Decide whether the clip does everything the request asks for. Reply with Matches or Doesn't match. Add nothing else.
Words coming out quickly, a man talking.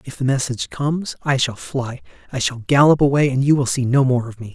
Matches